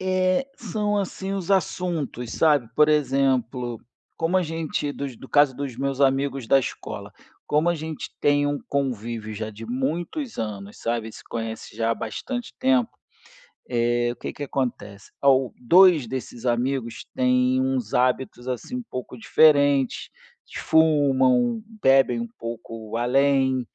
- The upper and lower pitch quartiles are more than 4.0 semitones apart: Yes, average, 4.6 semitones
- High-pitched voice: No, low, 135 Hz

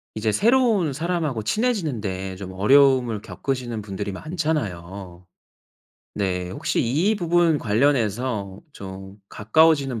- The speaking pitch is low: Yes, low, 120 Hz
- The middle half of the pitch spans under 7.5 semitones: No, wide, 8.0 semitones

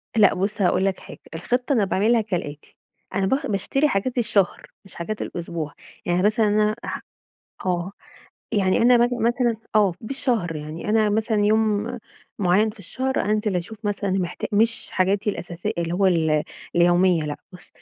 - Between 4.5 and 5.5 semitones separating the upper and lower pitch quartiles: No, average, 3.7 semitones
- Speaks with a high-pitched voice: Yes, high, 205 Hz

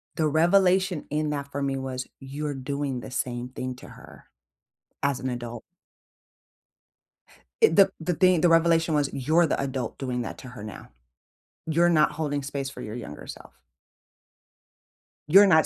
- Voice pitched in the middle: Yes, medium, 145 Hz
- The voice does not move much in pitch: No, average, 4.2 semitones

